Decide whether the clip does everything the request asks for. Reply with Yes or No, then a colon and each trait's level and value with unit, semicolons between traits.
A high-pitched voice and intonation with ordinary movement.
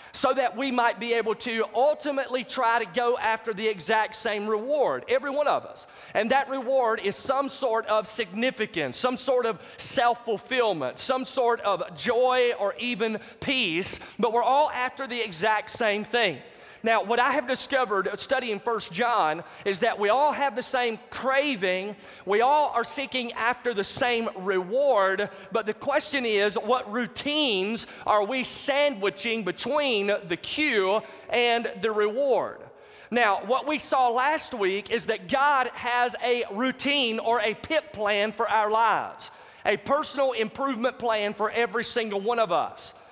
Yes: high, 235 Hz; average, 3.5 semitones